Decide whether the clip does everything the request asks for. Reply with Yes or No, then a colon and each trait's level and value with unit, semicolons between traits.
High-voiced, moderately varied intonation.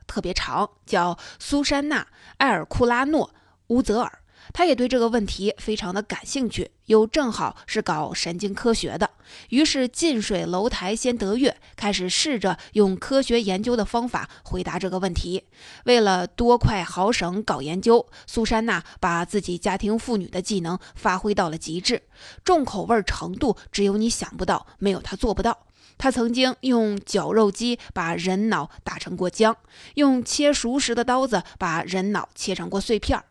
Yes: high, 215 Hz; average, 4.3 semitones